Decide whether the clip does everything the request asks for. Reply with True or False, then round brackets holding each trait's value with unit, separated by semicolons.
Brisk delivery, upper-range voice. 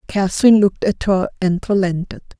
False (150 wpm; 195 Hz)